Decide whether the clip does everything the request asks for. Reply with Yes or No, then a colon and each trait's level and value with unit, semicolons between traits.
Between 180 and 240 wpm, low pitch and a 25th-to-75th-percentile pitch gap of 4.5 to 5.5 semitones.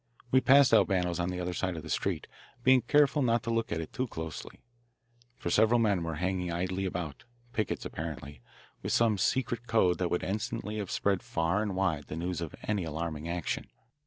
Yes: average, 195 wpm; very low, 90 Hz; average, 4.8 semitones